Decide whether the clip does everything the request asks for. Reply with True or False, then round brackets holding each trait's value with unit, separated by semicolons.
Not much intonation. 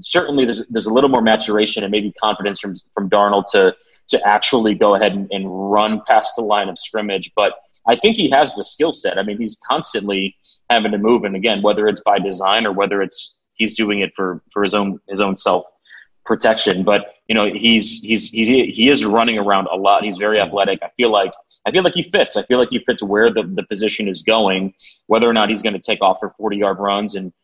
True (2.2 semitones)